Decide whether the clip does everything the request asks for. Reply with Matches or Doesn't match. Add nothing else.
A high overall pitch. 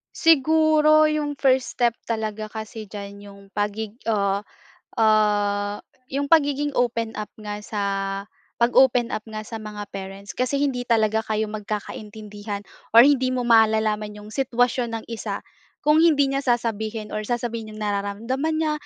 Matches